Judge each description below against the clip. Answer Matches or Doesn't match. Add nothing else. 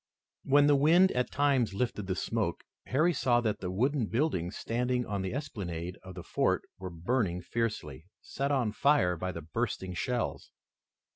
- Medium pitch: Doesn't match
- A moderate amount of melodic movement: Doesn't match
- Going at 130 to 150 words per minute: Doesn't match